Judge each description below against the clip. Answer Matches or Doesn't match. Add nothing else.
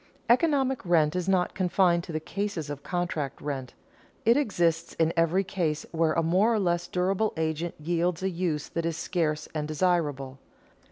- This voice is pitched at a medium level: Matches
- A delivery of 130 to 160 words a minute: Doesn't match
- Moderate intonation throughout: Matches